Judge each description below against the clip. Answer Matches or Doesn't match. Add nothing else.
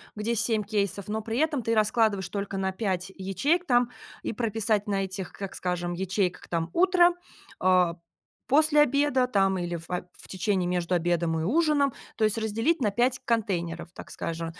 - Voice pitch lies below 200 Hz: Doesn't match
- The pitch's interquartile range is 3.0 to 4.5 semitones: Doesn't match